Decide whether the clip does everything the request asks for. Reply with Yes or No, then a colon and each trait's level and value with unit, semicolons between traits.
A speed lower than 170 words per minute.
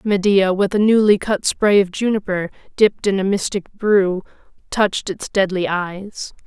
Yes: average, 160 wpm